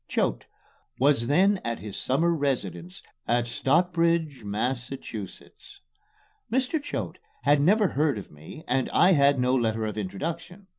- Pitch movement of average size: No, wide, 6.7 semitones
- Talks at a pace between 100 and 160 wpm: Yes, slow, 135 wpm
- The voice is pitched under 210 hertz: Yes, low, 135 Hz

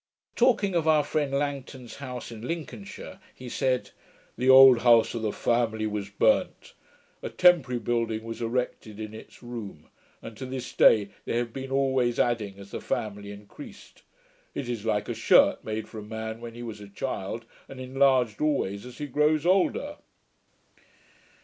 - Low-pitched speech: Yes, low, 120 Hz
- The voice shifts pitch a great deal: No, average, 3.6 semitones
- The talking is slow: No, average, 170 wpm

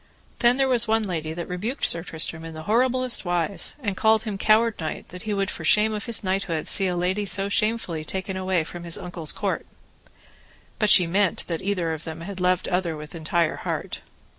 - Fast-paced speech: Yes, fast, 215 wpm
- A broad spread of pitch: No, average, 4.1 semitones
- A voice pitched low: No, medium, 185 Hz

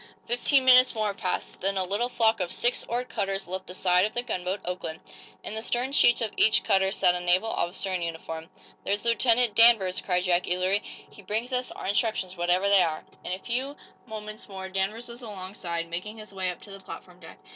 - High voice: Yes, high, 195 Hz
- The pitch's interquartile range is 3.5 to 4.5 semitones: Yes, average, 3.9 semitones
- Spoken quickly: Yes, fast, 215 wpm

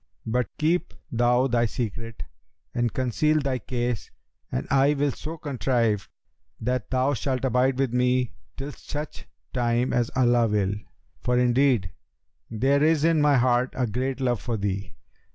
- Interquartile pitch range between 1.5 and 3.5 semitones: Yes, narrow, 2.5 semitones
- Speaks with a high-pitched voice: No, low, 125 Hz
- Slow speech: No, average, 150 wpm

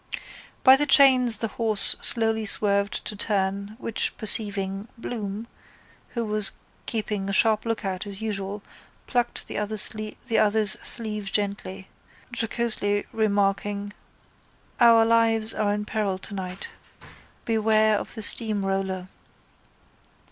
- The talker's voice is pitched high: Yes, high, 210 Hz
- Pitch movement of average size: No, narrow, 2.0 semitones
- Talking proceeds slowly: Yes, slow, 110 wpm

